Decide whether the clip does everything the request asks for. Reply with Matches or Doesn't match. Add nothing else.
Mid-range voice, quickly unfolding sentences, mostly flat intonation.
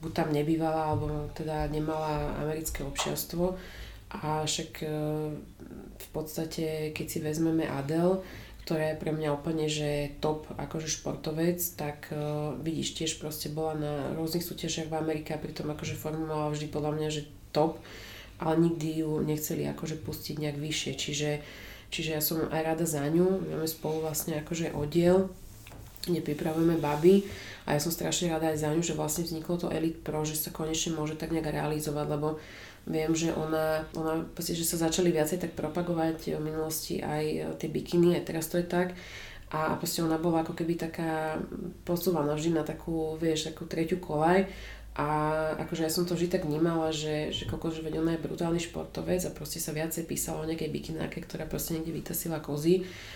Matches